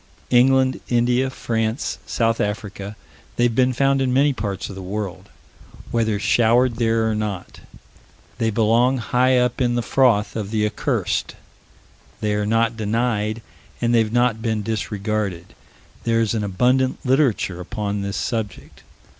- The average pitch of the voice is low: Yes, low, 115 Hz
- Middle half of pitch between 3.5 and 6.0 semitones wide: No, average, 2.8 semitones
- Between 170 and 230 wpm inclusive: No, average, 145 wpm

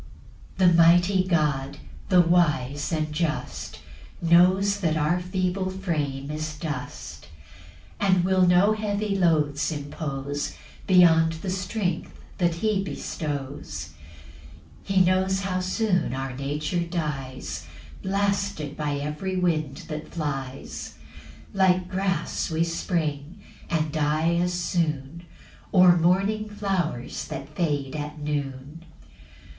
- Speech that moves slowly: Yes, slow, 115 wpm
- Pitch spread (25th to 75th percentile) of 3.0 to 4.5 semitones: Yes, average, 3.8 semitones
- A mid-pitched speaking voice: Yes, medium, 170 Hz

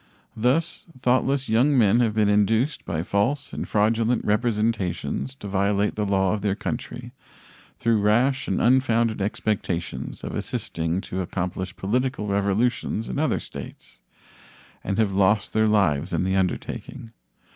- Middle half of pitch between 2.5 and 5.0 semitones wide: Yes, average, 3.5 semitones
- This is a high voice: No, low, 105 Hz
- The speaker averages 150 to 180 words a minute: No, average, 140 wpm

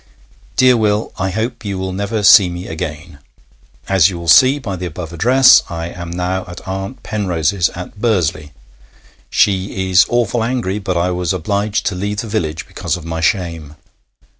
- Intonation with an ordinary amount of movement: Yes, average, 3.3 semitones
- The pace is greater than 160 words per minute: Yes, average, 175 wpm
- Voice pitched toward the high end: No, very low, 95 Hz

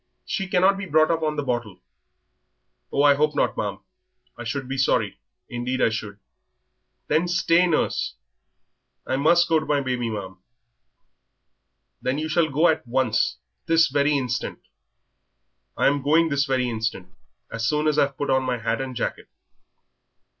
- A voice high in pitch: No, medium, 140 Hz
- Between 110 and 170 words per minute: Yes, average, 160 wpm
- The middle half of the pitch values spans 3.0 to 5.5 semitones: Yes, average, 4.2 semitones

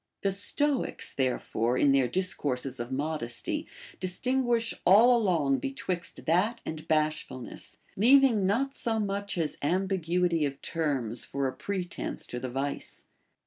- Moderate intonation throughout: No, wide, 6.8 semitones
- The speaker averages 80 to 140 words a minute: Yes, slow, 135 wpm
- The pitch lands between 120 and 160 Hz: No, medium, 175 Hz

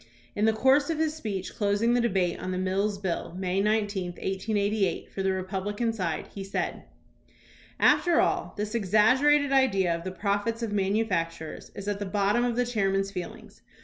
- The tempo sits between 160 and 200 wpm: Yes, average, 180 wpm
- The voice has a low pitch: No, high, 205 Hz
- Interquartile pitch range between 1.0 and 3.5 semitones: Yes, average, 3.1 semitones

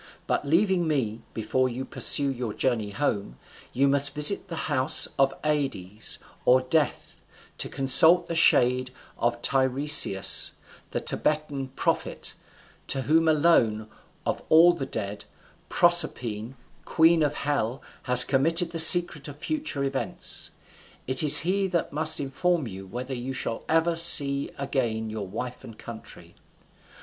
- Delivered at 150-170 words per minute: No, average, 140 wpm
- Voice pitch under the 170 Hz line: Yes, medium, 140 Hz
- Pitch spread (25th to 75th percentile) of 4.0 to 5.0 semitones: Yes, average, 4.6 semitones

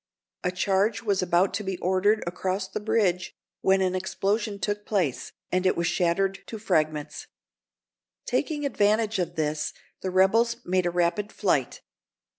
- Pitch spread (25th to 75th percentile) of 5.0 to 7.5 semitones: No, average, 2.7 semitones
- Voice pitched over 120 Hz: Yes, high, 190 Hz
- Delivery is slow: No, average, 150 wpm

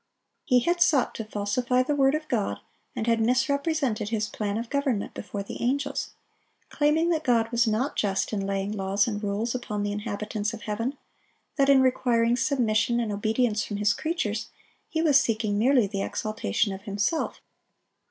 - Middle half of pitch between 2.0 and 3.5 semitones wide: No, average, 4.3 semitones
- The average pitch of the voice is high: Yes, high, 230 Hz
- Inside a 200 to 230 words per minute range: No, average, 170 wpm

